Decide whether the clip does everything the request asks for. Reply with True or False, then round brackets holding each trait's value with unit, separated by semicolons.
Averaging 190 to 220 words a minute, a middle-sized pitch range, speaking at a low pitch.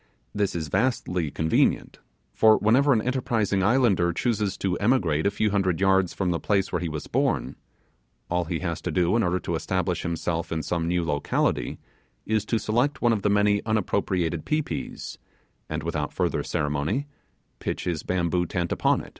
False (180 wpm; 4.3 semitones; 95 Hz)